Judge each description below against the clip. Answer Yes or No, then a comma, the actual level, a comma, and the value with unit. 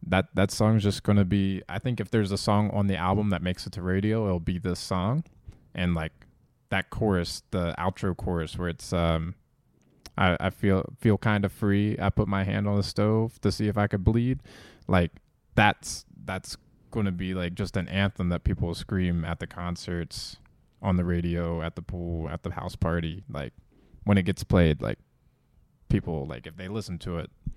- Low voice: Yes, very low, 95 Hz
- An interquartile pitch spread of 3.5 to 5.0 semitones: No, average, 2.8 semitones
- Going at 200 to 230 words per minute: Yes, fast, 205 wpm